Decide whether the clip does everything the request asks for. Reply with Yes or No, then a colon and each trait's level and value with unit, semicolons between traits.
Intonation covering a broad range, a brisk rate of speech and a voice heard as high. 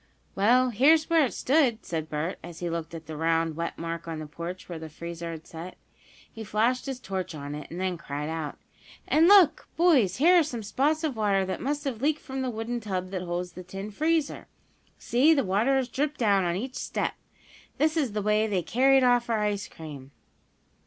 Yes: wide, 7.8 semitones; fast, 215 wpm; high, 210 Hz